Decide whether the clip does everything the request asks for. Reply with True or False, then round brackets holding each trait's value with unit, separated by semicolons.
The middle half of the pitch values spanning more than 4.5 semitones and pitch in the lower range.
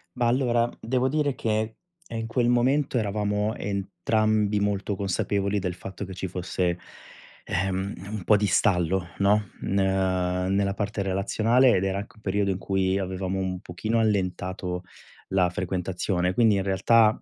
False (2.6 semitones; 100 Hz)